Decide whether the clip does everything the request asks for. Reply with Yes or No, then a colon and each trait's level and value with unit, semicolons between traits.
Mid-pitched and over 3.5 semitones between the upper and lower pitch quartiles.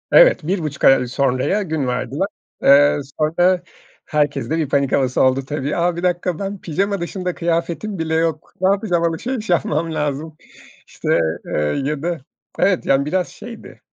Yes: medium, 165 Hz; average, 4.0 semitones